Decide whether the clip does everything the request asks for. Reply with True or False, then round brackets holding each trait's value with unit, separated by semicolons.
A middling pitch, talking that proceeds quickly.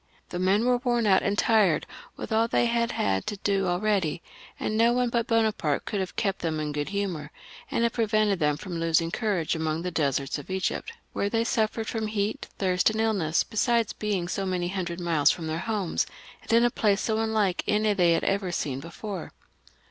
False (195 Hz; 210 wpm)